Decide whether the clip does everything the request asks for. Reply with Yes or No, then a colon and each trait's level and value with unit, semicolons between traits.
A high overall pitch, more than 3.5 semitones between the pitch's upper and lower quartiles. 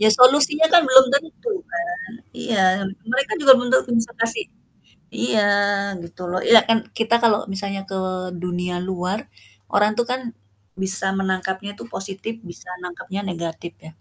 Yes: high, 210 Hz; average, 5.2 semitones